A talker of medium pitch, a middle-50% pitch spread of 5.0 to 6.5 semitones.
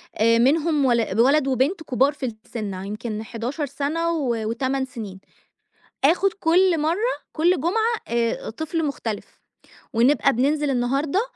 No: very high, 275 Hz; wide, 5.4 semitones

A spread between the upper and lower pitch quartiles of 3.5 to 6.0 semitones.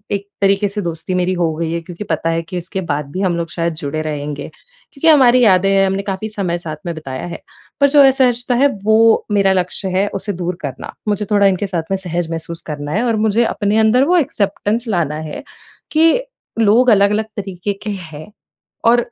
Yes: average, 4.4 semitones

